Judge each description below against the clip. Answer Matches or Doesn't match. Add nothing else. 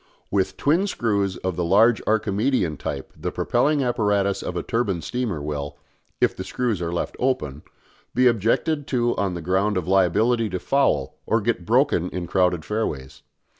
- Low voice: Matches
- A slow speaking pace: Doesn't match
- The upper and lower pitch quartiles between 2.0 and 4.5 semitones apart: Doesn't match